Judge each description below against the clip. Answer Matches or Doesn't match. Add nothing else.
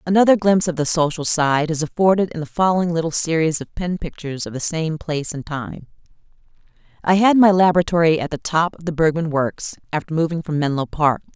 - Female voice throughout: Matches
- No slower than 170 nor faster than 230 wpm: Matches